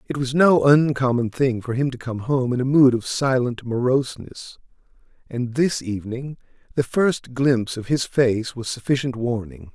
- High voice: No, low, 125 Hz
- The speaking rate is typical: Yes, average, 170 wpm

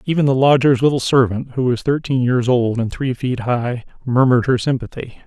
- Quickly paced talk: No, average, 195 wpm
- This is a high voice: No, low, 125 Hz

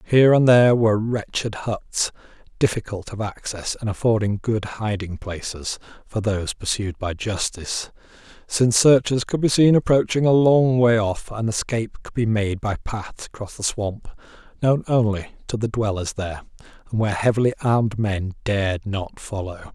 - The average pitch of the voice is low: Yes, low, 110 Hz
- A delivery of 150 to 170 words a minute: Yes, average, 160 wpm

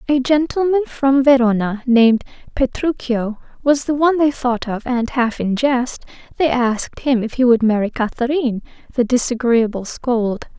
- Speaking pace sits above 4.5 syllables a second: Yes, 4.7 syllables/s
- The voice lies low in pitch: No, very high, 250 Hz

